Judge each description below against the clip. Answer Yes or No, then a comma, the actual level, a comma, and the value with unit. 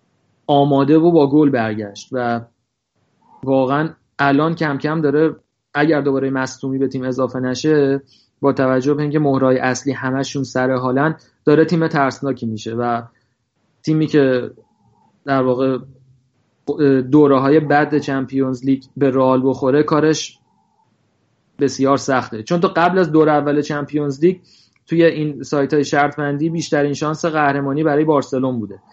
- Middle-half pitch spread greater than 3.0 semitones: No, narrow, 2.6 semitones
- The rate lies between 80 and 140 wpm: Yes, average, 135 wpm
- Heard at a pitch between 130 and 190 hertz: Yes, medium, 140 Hz